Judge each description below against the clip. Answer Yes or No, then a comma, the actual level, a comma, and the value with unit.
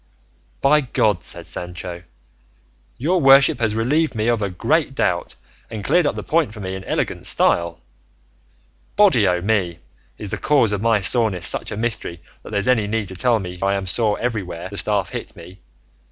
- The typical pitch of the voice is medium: No, low, 105 Hz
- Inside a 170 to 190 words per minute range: Yes, average, 185 wpm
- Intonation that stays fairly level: No, average, 4.3 semitones